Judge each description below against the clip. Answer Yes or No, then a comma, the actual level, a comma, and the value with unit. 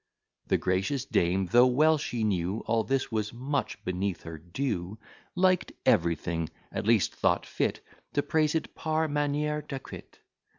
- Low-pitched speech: Yes, low, 120 Hz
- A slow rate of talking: No, average, 145 wpm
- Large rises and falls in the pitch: Yes, wide, 8.0 semitones